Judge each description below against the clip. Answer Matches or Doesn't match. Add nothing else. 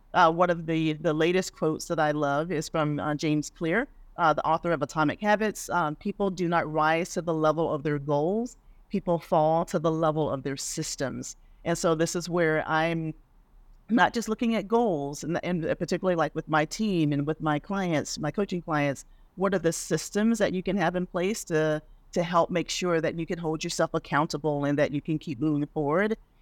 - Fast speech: Matches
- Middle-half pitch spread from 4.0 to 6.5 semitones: Doesn't match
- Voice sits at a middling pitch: Matches